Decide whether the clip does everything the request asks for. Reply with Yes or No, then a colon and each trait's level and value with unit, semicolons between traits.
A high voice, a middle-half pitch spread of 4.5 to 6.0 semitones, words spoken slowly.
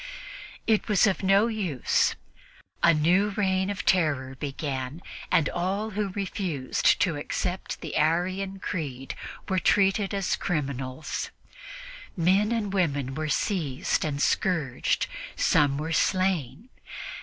No: medium, 175 Hz; average, 5.1 semitones; slow, 120 wpm